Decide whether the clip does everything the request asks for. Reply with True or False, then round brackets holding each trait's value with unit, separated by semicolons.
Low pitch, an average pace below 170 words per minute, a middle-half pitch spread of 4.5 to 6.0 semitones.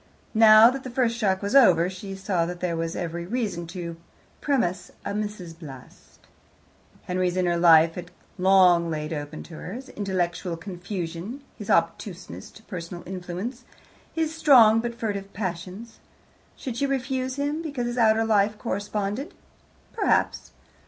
False (195 Hz; 145 wpm; 5.1 semitones)